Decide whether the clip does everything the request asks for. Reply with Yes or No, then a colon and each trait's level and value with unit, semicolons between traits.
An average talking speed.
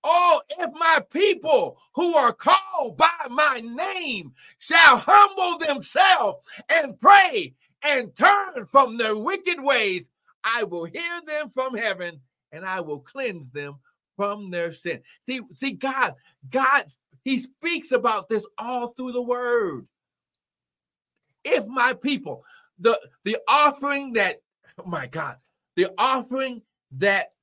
No: slow, 130 wpm